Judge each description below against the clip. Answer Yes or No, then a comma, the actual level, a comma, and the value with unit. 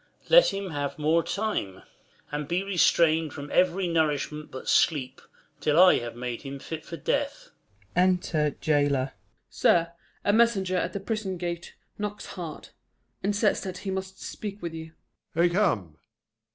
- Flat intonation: No, average, 4.3 semitones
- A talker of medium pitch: Yes, medium, 170 Hz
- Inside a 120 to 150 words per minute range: No, average, 160 wpm